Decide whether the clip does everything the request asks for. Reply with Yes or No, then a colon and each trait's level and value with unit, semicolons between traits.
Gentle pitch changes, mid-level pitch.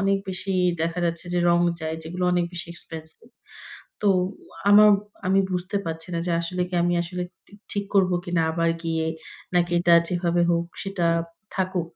Yes: narrow, 1.8 semitones; medium, 175 Hz